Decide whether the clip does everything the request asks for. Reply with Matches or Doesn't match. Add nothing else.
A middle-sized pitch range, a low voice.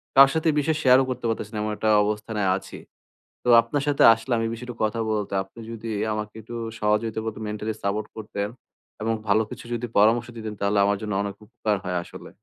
Doesn't match